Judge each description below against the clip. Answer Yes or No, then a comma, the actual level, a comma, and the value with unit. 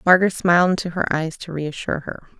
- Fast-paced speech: Yes, fast, 225 wpm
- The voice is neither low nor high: Yes, medium, 170 Hz